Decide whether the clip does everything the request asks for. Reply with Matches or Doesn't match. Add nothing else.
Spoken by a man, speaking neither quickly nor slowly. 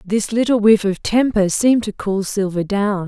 Doesn't match